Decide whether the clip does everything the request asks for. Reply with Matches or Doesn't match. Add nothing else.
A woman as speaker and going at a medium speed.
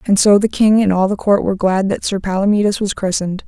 Doesn't match